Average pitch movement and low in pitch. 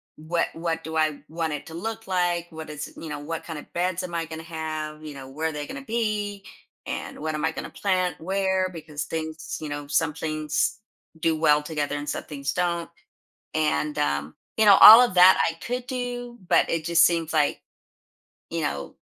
No: average, 3.2 semitones; medium, 165 Hz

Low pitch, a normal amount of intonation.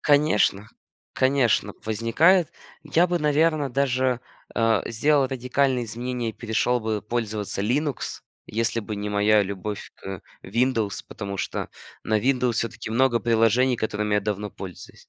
Yes: low, 115 Hz; average, 3.8 semitones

